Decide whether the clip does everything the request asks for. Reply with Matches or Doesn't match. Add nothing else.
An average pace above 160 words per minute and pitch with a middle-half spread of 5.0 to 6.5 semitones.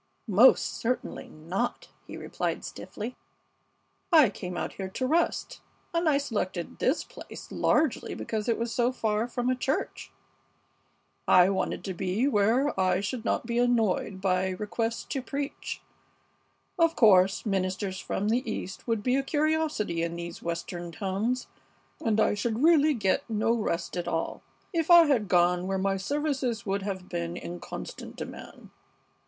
Doesn't match